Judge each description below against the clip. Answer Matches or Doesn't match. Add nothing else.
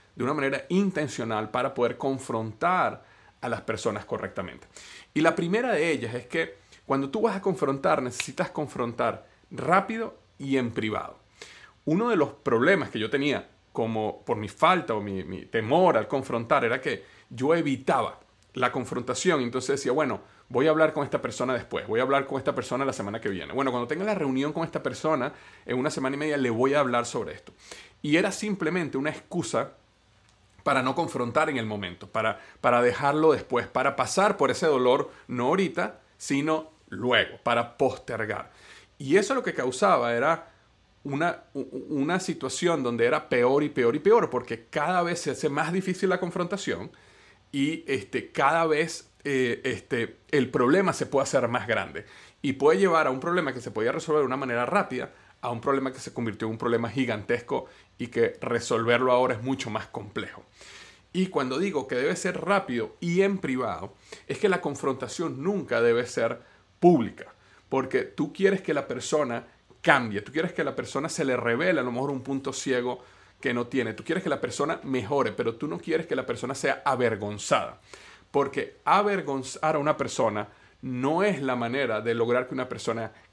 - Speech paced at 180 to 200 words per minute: Matches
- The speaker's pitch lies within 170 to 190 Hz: Doesn't match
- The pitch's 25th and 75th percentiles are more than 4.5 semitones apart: Matches